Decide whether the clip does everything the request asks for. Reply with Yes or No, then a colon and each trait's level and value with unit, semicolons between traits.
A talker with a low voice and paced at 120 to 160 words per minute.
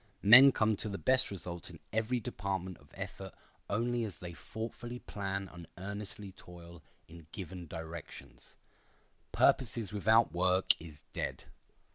Yes: very low, 95 Hz; slow, 135 wpm